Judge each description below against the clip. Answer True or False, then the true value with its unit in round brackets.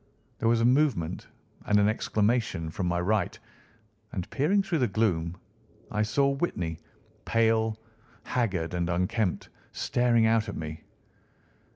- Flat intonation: False (4.9 semitones)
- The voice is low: True (110 Hz)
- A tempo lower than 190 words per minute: True (135 wpm)